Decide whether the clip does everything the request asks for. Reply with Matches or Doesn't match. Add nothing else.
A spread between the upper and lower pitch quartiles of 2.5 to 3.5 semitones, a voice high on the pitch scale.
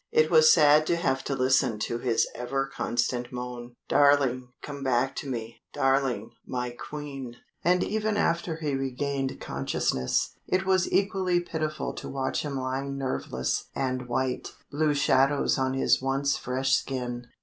Doesn't match